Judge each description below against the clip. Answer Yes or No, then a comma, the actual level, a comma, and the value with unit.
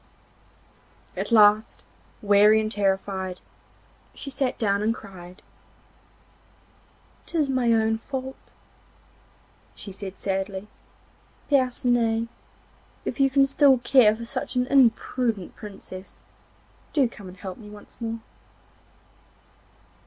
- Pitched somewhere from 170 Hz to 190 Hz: No, high, 220 Hz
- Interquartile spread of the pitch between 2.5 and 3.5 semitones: No, average, 4.0 semitones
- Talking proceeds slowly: Yes, slow, 110 wpm